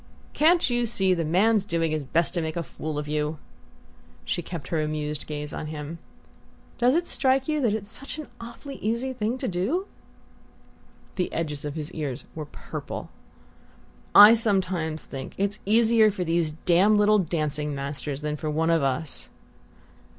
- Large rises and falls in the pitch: Yes, wide, 6.3 semitones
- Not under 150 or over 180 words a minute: Yes, average, 170 wpm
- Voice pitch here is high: No, medium, 170 Hz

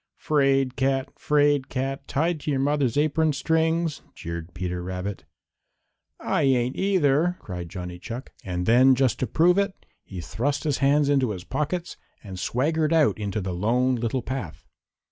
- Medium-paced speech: Yes, average, 160 wpm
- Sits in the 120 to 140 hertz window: Yes, low, 135 Hz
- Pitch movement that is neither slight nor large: No, wide, 6.0 semitones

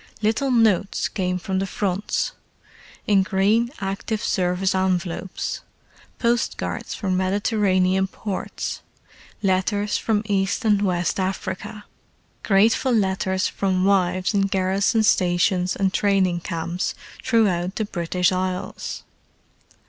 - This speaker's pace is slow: Yes, slow, 105 wpm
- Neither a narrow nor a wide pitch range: No, narrow, 2.0 semitones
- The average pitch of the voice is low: No, high, 190 Hz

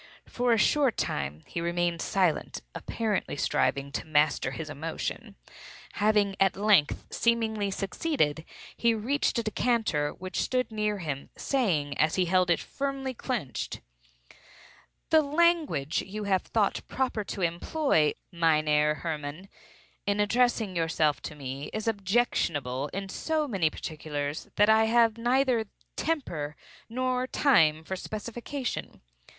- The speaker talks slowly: Yes, slow, 125 wpm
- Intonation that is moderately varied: No, wide, 7.3 semitones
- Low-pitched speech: No, high, 195 Hz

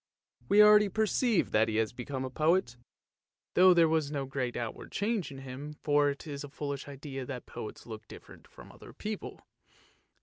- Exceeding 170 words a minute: Yes, average, 190 wpm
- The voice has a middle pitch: Yes, medium, 145 Hz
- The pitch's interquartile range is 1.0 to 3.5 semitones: No, wide, 5.4 semitones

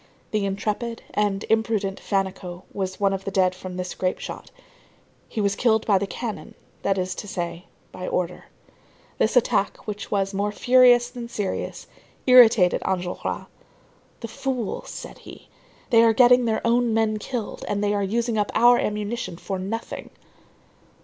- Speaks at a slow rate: No, average, 155 wpm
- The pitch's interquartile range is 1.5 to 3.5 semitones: Yes, average, 3.2 semitones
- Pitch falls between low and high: No, high, 210 Hz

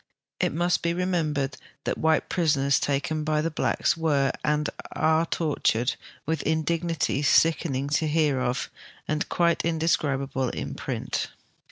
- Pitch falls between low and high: Yes, medium, 155 Hz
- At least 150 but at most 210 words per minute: No, slow, 135 wpm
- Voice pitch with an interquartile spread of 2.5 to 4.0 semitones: Yes, average, 2.8 semitones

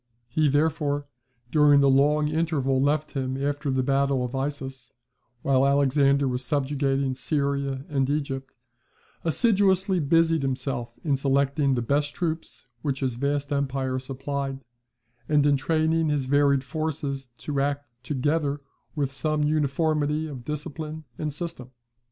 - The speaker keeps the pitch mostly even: Yes, narrow, 2.0 semitones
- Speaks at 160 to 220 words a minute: No, slow, 135 wpm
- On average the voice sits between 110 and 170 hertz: Yes, medium, 140 Hz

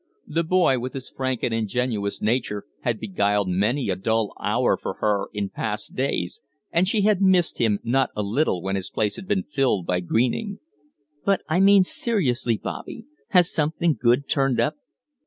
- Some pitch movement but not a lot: No, wide, 8.3 semitones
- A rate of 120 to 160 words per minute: No, average, 175 wpm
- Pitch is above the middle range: No, low, 125 Hz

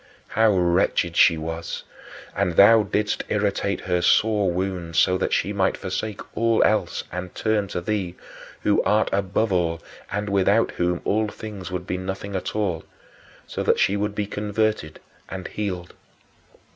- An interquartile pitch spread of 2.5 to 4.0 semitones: Yes, average, 2.8 semitones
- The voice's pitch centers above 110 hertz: No, low, 100 Hz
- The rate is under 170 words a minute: Yes, average, 160 wpm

